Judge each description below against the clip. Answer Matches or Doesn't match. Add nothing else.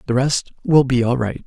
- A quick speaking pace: Matches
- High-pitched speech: Doesn't match